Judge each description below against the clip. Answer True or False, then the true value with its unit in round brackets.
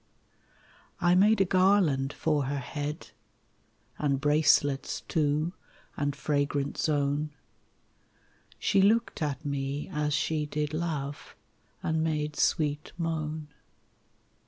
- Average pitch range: False (1.9 semitones)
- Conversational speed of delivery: False (105 wpm)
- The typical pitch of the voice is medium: True (150 Hz)